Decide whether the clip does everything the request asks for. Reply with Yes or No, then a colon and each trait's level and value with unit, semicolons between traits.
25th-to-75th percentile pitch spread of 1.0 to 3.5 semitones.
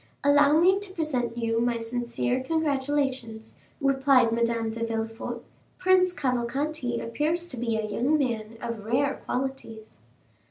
No: average, 3.9 semitones